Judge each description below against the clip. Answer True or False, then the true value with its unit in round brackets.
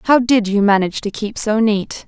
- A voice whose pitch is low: False (215 Hz)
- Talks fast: True (230 wpm)